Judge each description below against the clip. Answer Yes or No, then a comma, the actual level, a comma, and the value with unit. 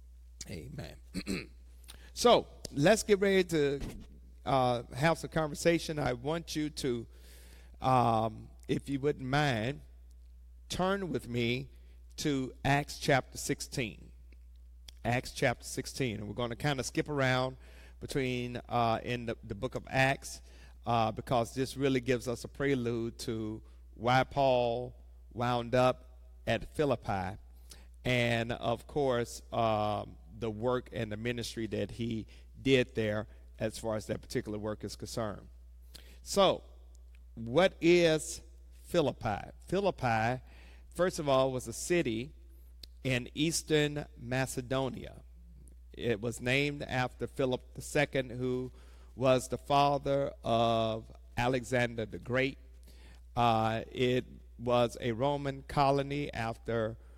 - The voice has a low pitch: Yes, low, 120 Hz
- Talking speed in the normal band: No, slow, 120 wpm